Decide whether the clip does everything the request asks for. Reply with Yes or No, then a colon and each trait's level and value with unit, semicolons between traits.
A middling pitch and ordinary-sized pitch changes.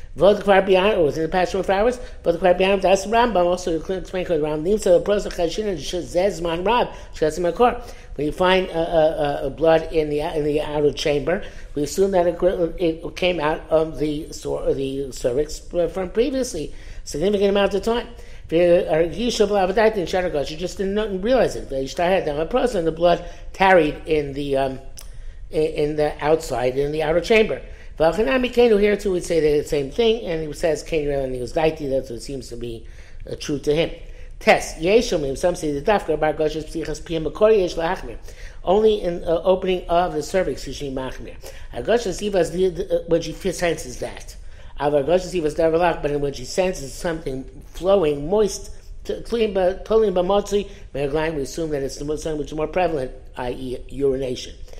Yes: medium, 165 Hz; average, 4.3 semitones